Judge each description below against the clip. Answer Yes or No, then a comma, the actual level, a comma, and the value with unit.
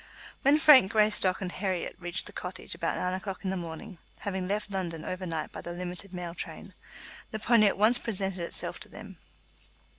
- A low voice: No, high, 190 Hz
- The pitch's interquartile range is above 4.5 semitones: No, average, 2.8 semitones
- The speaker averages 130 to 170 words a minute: No, average, 190 wpm